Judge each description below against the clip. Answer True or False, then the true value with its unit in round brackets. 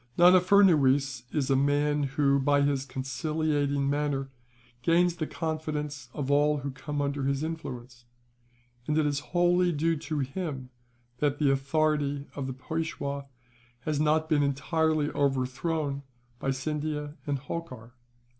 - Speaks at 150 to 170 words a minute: False (135 wpm)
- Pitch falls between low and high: True (145 Hz)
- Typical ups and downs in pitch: False (2.2 semitones)